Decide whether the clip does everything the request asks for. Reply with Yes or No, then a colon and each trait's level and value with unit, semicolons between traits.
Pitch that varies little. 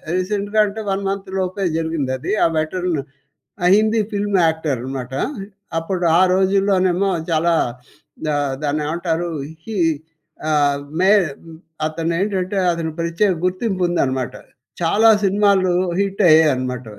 No: average, 3.7 semitones